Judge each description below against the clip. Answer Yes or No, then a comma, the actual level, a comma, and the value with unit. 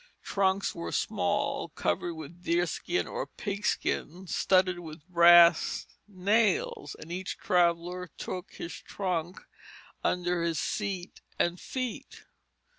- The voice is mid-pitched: Yes, medium, 180 Hz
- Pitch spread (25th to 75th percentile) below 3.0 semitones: Yes, narrow, 2.5 semitones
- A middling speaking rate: No, slow, 110 wpm